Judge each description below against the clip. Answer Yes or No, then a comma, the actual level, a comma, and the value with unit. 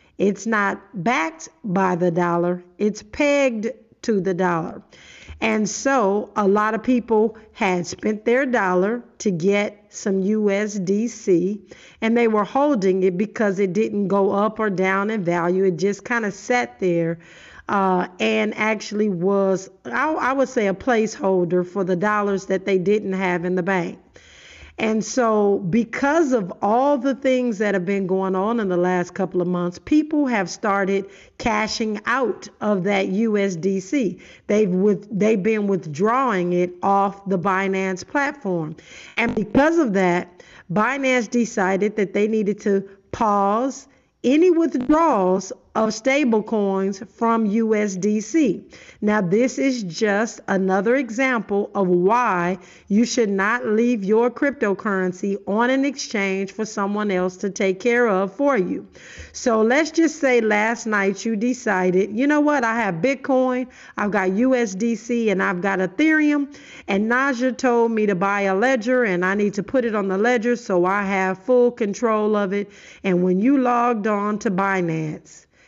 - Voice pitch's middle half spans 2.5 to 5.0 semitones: Yes, average, 3.7 semitones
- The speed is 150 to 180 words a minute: Yes, average, 155 wpm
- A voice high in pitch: Yes, high, 210 Hz